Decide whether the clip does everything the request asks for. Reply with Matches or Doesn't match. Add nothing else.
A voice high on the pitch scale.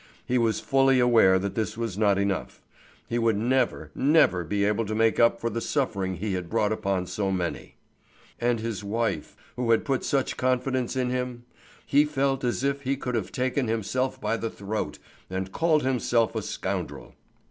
Doesn't match